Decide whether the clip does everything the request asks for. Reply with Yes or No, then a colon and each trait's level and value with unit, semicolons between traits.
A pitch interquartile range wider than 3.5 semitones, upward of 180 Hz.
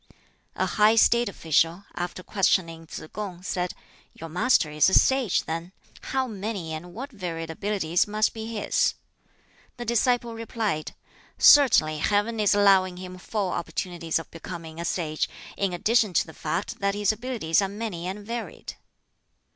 Yes: average, 4.6 semitones; high, 190 Hz